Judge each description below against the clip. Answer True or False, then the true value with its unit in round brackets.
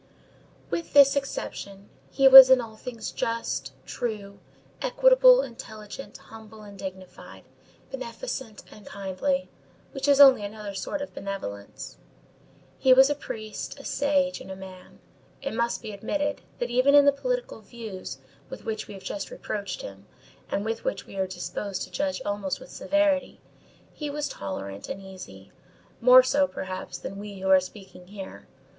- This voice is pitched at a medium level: False (220 Hz)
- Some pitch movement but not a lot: False (6.0 semitones)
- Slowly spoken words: False (155 wpm)